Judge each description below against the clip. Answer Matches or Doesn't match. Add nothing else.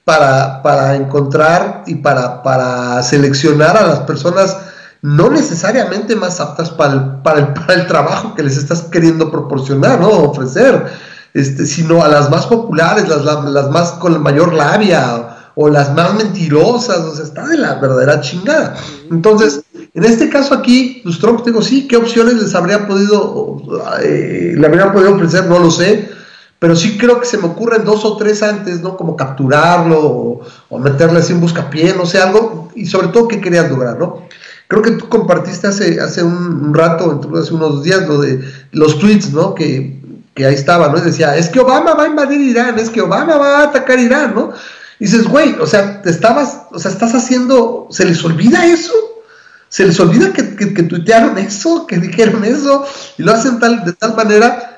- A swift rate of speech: Matches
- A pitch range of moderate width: Doesn't match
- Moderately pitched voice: Matches